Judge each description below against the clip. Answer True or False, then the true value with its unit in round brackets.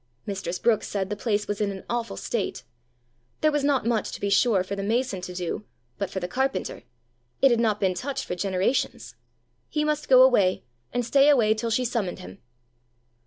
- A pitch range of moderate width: True (4.6 semitones)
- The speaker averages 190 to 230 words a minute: True (200 wpm)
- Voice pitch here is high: True (215 Hz)